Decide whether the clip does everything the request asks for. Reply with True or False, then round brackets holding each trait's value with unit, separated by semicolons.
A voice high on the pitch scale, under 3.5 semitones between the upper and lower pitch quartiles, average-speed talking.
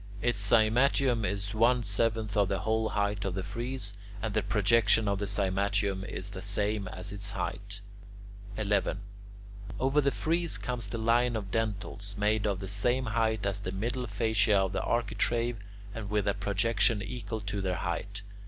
False (105 Hz; 2.4 semitones; 170 wpm)